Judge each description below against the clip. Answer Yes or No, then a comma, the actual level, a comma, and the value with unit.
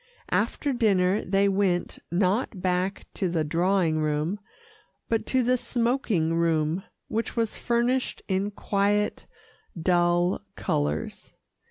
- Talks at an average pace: No, slow, 115 wpm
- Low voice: No, high, 190 Hz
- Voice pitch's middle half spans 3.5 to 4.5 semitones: Yes, average, 3.9 semitones